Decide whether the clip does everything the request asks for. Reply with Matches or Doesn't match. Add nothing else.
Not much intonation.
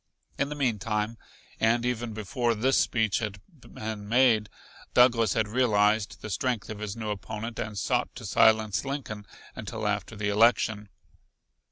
Matches